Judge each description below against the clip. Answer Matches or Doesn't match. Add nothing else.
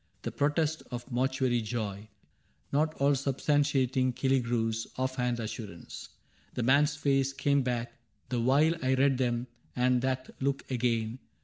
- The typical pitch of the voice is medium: Doesn't match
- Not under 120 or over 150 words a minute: Matches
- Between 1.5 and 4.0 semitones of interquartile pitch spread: Matches